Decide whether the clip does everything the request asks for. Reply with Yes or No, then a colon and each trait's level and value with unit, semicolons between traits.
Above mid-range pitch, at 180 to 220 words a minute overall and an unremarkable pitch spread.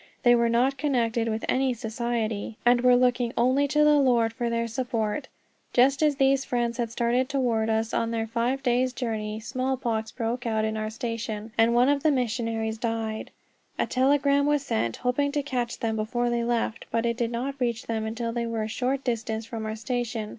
No: high, 235 Hz; average, 200 wpm; narrow, 2.3 semitones